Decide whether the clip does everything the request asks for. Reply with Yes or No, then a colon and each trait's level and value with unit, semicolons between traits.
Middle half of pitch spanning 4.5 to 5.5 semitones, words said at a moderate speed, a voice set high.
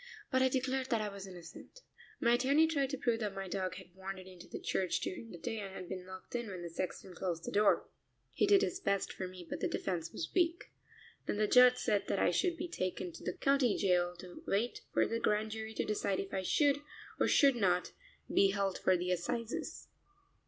No: average, 5.2 semitones; fast, 225 wpm; high, 200 Hz